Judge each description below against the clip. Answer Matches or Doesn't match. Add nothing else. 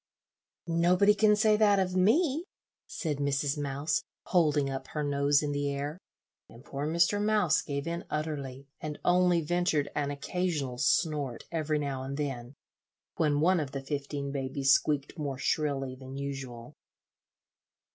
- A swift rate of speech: Doesn't match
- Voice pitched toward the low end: Doesn't match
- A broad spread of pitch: Doesn't match